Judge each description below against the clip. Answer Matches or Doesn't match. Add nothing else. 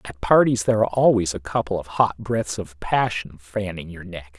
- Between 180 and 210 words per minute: Matches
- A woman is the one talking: Doesn't match